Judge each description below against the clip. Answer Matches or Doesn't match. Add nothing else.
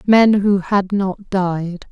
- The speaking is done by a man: Doesn't match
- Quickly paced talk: Doesn't match